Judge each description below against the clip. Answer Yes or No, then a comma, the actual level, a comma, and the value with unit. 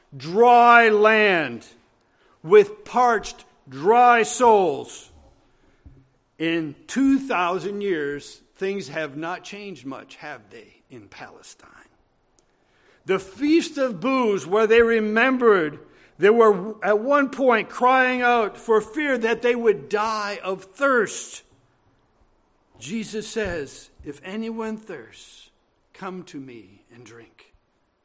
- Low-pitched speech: No, high, 220 Hz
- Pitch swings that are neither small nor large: Yes, average, 4.2 semitones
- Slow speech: Yes, slow, 105 wpm